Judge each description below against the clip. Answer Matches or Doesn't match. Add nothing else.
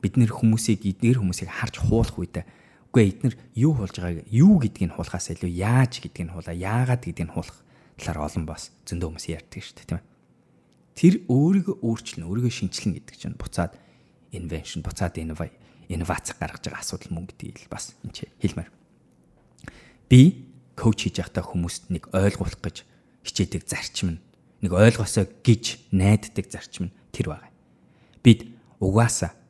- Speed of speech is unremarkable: Matches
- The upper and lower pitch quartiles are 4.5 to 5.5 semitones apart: Matches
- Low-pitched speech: Matches